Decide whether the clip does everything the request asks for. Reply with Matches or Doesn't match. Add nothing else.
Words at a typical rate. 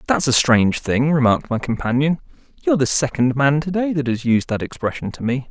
Doesn't match